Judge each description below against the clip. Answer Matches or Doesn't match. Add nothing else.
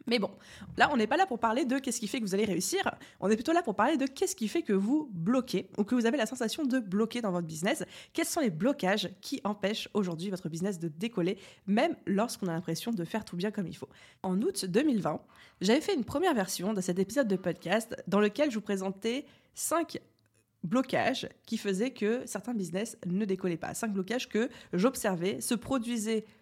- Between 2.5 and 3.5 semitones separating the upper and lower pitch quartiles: Doesn't match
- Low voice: Doesn't match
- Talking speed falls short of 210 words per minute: Doesn't match